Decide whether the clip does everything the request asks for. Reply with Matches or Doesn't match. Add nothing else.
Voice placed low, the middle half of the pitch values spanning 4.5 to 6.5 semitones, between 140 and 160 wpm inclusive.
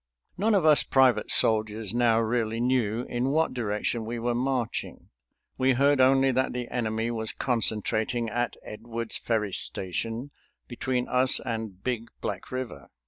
Doesn't match